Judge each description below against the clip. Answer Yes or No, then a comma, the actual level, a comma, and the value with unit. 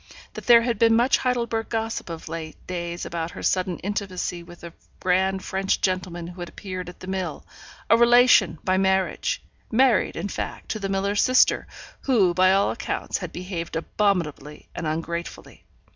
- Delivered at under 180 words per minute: Yes, average, 170 wpm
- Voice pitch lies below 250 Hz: Yes, high, 190 Hz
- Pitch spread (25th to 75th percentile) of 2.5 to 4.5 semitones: Yes, average, 3.9 semitones